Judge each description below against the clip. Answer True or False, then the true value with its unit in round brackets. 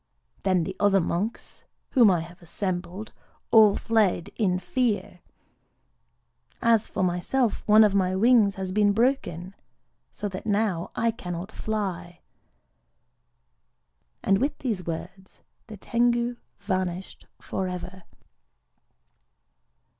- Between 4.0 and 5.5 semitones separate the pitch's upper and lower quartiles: False (3.3 semitones)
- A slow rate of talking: True (110 wpm)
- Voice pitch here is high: True (195 Hz)